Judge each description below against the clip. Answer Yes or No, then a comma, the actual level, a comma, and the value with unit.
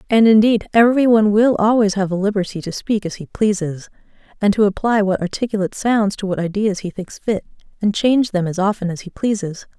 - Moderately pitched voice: No, high, 205 Hz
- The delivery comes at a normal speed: No, fast, 210 wpm